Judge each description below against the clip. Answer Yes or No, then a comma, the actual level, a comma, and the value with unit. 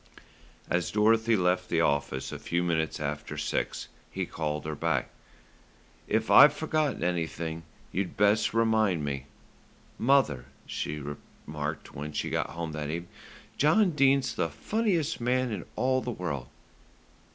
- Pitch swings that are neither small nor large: No, wide, 8.3 semitones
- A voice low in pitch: Yes, very low, 90 Hz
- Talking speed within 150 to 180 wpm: No, average, 140 wpm